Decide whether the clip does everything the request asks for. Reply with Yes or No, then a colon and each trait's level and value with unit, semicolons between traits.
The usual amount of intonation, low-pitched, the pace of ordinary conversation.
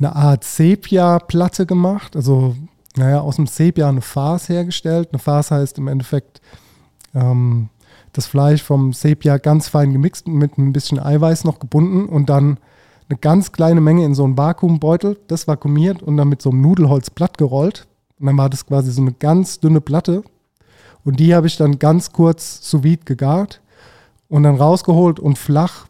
No: average, 3.1 semitones; medium, 150 Hz; average, 175 wpm